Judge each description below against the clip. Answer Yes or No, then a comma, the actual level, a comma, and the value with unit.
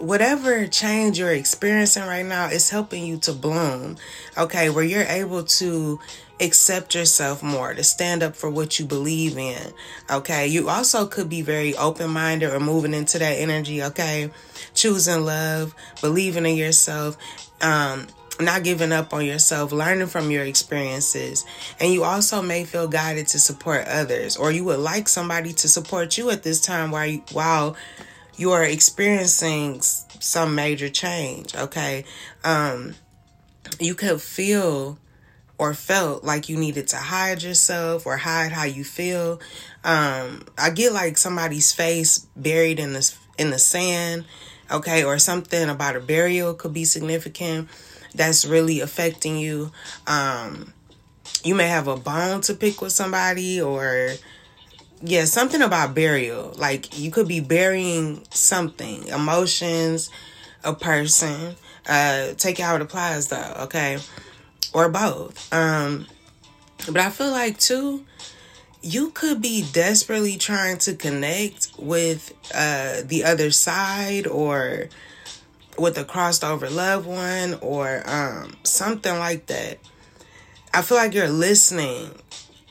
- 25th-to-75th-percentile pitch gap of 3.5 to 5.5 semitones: No, average, 3.1 semitones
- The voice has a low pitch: No, medium, 160 Hz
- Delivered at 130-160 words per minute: Yes, average, 140 wpm